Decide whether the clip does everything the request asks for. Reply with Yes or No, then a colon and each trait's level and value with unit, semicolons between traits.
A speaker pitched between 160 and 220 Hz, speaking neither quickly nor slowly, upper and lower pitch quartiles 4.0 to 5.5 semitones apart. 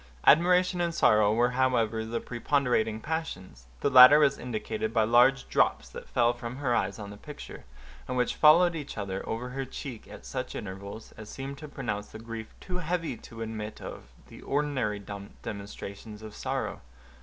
No: low, 120 Hz; average, 175 wpm; average, 4.4 semitones